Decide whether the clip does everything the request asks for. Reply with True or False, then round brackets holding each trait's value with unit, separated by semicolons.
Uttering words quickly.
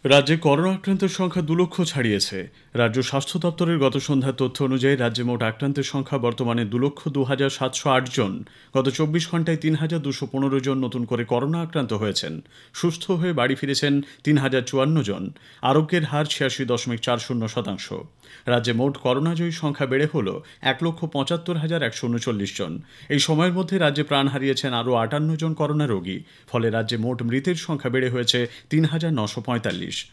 True (180 wpm)